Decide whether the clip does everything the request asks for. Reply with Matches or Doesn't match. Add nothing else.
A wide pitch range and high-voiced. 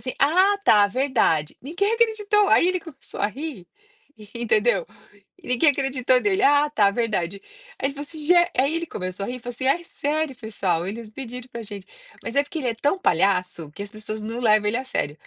Matches